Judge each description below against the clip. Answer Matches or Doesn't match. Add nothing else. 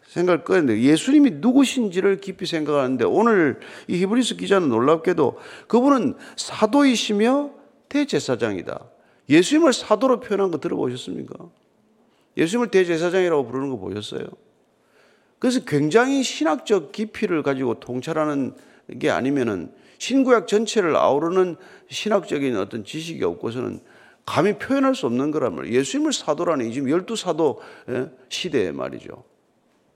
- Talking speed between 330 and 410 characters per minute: Matches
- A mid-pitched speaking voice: Doesn't match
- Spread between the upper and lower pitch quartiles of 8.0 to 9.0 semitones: Matches